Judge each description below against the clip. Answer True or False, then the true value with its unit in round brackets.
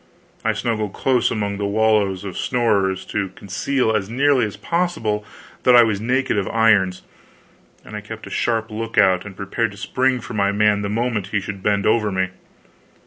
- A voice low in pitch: True (105 Hz)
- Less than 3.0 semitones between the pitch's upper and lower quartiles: True (2.6 semitones)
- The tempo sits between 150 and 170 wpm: False (185 wpm)